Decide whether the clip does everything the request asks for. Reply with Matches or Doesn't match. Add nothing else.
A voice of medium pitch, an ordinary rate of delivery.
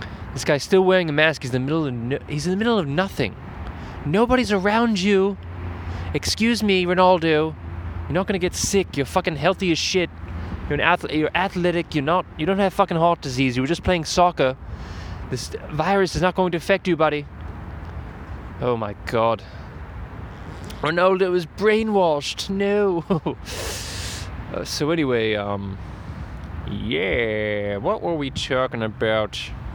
Matches